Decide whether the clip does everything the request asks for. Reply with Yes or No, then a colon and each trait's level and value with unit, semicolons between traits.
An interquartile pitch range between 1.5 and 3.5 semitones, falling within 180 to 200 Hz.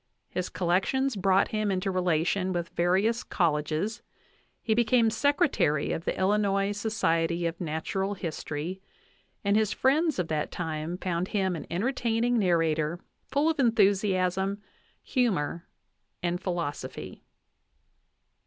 No: average, 4.3 semitones; high, 190 Hz